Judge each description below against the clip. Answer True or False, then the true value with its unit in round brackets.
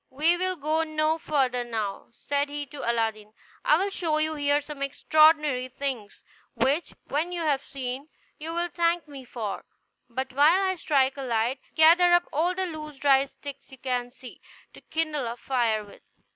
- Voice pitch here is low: False (285 Hz)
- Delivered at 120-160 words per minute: False (180 wpm)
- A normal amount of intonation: True (3.7 semitones)